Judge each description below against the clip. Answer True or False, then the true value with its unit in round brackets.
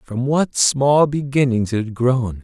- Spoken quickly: False (175 wpm)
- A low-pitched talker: True (130 Hz)